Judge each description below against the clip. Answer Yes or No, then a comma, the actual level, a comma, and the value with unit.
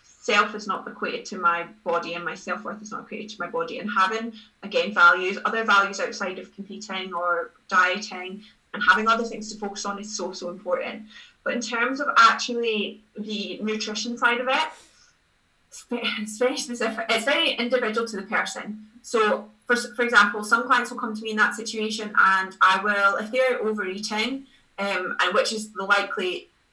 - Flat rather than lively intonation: No, average, 3.1 semitones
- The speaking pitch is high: Yes, high, 215 Hz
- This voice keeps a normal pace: Yes, average, 190 wpm